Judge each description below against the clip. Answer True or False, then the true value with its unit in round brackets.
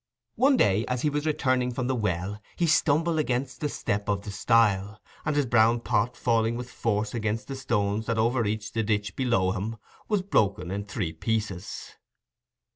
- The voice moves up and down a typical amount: True (3.8 semitones)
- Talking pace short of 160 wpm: False (180 wpm)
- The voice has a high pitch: False (115 Hz)